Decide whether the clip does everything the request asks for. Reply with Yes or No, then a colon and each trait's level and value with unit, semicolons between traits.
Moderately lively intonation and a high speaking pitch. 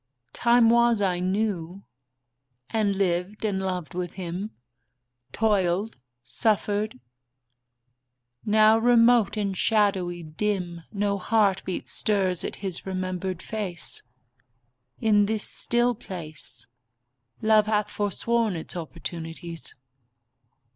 Yes: average, 3.3 semitones; high, 200 Hz